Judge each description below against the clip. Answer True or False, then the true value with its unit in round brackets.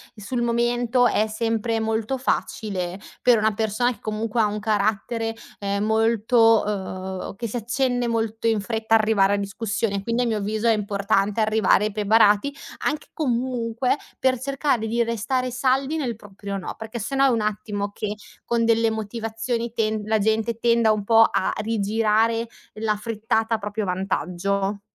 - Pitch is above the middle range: True (220 Hz)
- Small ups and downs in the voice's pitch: True (2.0 semitones)